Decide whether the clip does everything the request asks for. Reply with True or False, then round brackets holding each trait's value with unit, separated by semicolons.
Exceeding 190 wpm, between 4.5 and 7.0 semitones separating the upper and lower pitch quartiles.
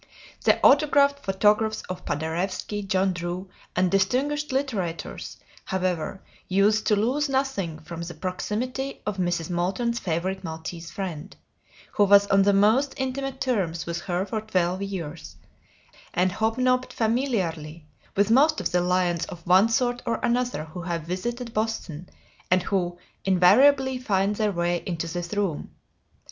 False (140 wpm; 5.2 semitones)